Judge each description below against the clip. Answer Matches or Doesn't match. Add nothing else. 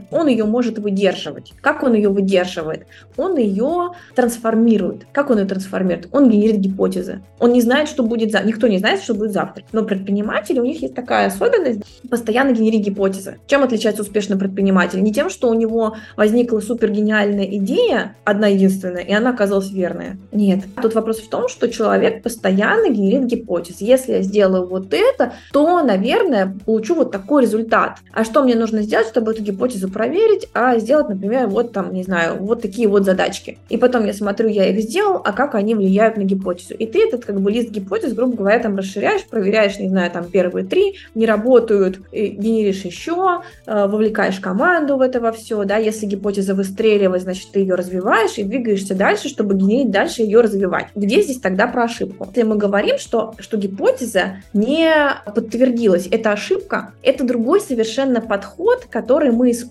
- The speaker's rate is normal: Doesn't match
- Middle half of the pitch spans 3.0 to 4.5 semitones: Matches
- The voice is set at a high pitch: Matches